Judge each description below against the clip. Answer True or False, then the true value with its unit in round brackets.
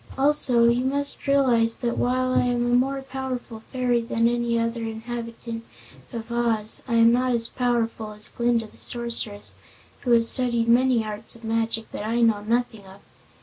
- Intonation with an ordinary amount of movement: False (1.5 semitones)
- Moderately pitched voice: False (235 Hz)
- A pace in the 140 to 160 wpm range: False (175 wpm)